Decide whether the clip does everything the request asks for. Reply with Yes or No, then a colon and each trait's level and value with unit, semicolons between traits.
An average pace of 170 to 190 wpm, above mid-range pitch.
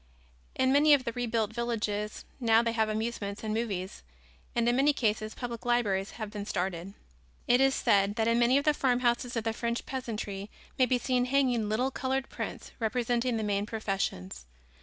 Yes: average, 180 wpm; high, 230 Hz